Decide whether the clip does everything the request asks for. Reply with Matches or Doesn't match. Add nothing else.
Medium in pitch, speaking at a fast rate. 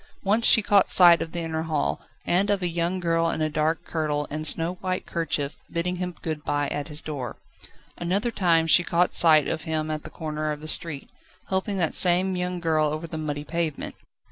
Matches